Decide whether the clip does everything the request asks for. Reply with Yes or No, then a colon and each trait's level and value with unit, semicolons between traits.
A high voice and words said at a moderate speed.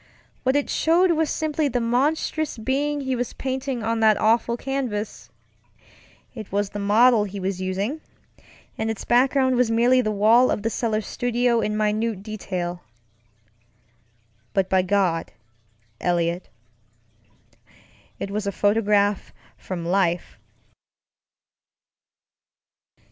No: high, 220 Hz; slow, 115 wpm